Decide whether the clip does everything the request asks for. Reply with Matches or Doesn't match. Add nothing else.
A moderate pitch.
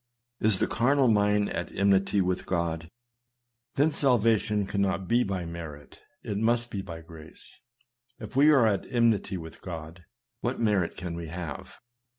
Doesn't match